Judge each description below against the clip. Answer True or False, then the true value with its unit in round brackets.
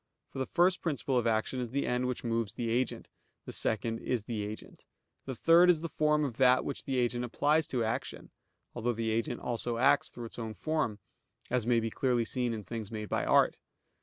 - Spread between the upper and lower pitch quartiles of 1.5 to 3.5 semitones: True (2.8 semitones)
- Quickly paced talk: True (215 wpm)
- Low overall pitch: True (120 Hz)